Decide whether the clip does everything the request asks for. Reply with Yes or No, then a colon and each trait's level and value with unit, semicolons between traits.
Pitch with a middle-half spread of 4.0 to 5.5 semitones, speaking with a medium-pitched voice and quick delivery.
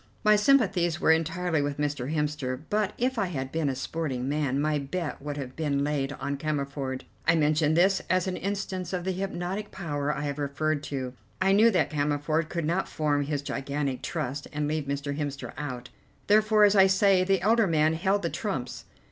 No: average, 4.6 semitones; medium, 155 Hz; average, 195 wpm